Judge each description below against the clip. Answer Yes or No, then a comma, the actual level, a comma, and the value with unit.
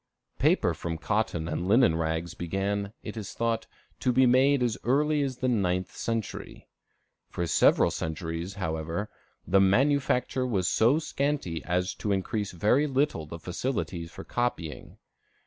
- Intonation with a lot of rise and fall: Yes, wide, 6.6 semitones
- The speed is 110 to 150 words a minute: Yes, average, 145 wpm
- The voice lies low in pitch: Yes, low, 100 Hz